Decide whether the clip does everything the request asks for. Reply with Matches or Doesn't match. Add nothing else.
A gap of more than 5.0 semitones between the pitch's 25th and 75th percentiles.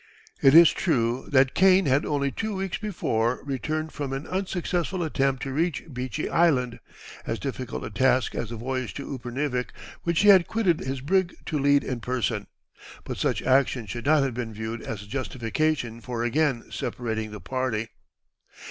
Doesn't match